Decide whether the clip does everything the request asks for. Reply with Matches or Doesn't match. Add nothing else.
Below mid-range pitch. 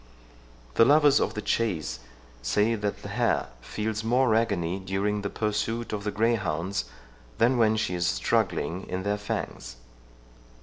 Matches